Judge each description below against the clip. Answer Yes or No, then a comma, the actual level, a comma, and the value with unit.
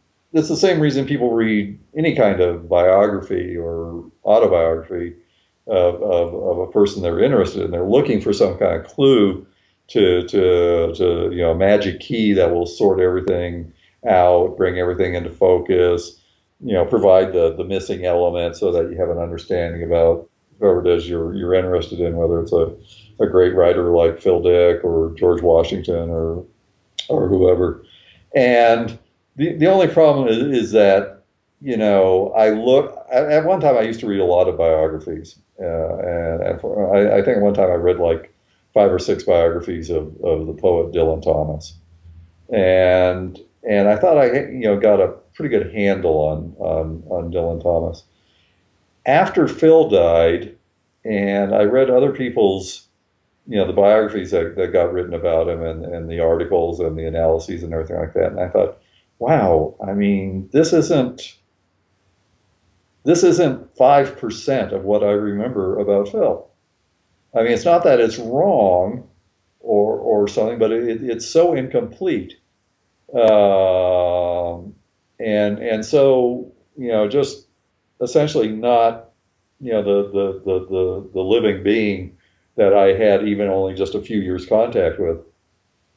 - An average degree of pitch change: Yes, average, 4.2 semitones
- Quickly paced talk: No, average, 165 wpm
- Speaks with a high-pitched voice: No, very low, 95 Hz